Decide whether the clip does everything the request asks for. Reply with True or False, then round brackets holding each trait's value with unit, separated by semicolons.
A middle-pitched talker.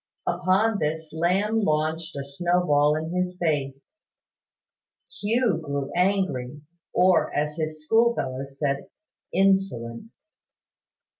True (160 Hz)